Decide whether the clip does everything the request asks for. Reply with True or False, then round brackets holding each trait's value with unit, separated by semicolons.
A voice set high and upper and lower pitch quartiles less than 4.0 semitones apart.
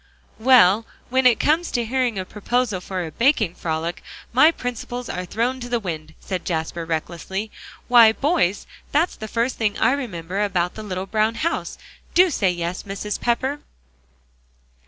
False (220 Hz; 5.4 semitones)